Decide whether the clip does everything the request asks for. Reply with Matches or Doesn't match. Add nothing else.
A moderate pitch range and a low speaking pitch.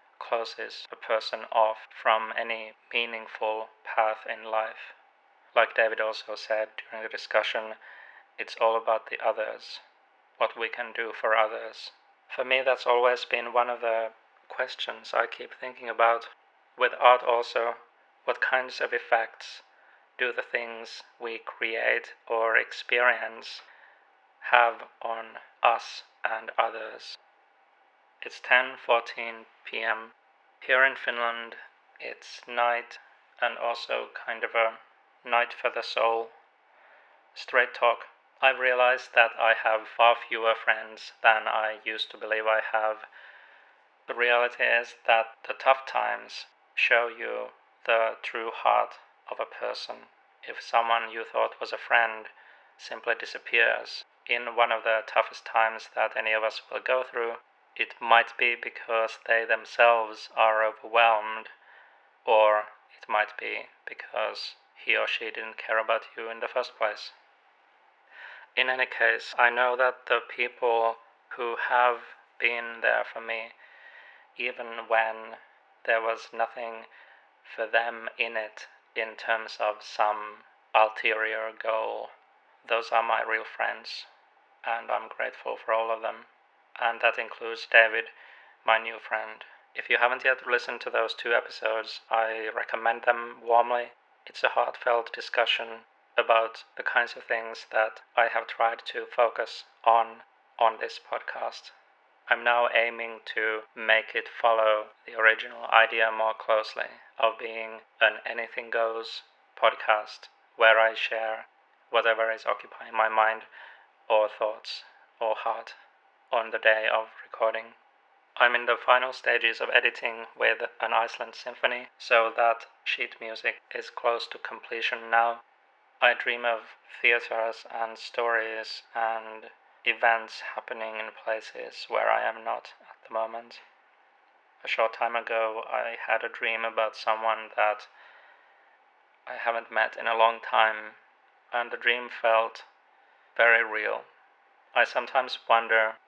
Doesn't match